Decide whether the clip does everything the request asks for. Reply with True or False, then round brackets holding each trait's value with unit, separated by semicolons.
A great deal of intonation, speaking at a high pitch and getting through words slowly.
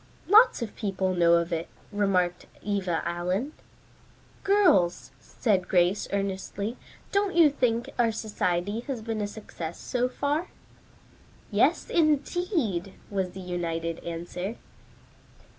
True (5.8 semitones; 200 Hz; 115 wpm)